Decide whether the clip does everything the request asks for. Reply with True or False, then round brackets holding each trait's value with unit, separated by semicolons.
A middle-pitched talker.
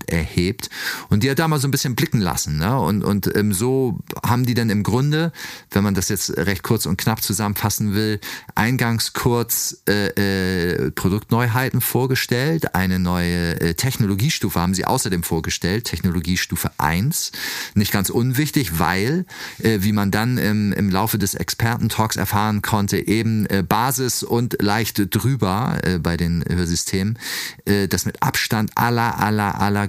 False (105 Hz)